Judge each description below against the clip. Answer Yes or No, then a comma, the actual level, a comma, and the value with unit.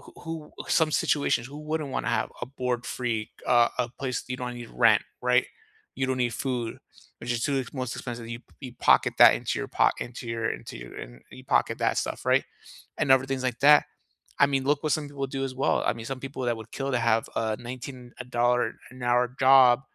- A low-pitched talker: Yes, low, 125 Hz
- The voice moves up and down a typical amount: No, narrow, 2.2 semitones